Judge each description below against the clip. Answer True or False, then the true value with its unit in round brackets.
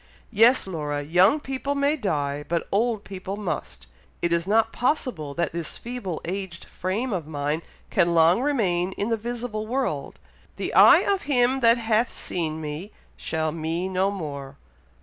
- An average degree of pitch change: False (6.5 semitones)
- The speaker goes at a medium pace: True (160 wpm)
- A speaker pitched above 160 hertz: True (190 Hz)